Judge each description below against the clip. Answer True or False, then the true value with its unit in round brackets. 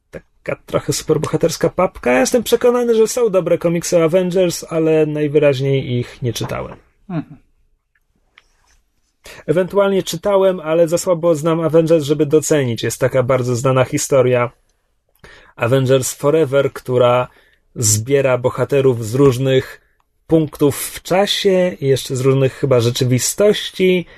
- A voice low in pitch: False (150 Hz)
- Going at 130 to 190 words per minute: False (115 wpm)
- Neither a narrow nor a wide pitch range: True (4.7 semitones)